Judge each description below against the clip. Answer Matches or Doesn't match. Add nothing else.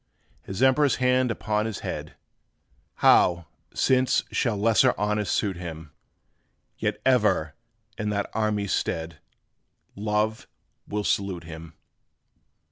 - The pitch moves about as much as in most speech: Matches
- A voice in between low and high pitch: Doesn't match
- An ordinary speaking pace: Doesn't match